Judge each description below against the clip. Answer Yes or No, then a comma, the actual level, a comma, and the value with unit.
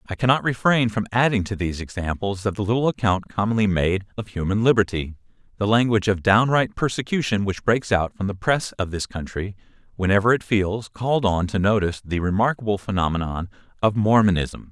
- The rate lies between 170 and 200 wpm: Yes, average, 175 wpm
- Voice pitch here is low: Yes, low, 105 Hz